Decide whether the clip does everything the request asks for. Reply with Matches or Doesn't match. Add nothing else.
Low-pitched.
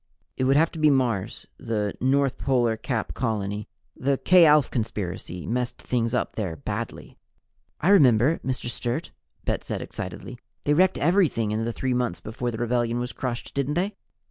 Matches